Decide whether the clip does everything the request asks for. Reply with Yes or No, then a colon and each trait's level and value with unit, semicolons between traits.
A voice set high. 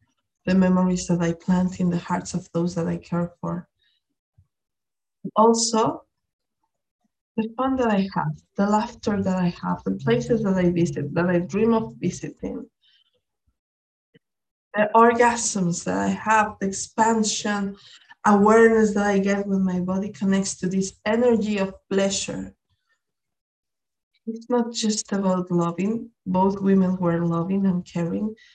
Yes: high, 195 Hz